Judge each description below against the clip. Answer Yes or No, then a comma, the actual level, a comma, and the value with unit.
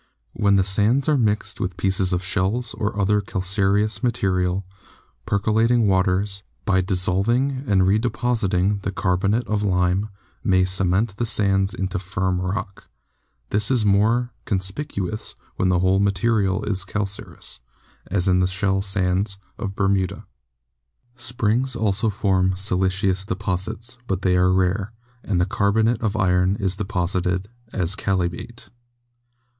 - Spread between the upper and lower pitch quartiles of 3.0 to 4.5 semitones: No, narrow, 2.4 semitones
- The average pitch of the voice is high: No, low, 100 Hz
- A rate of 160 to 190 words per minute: No, slow, 135 wpm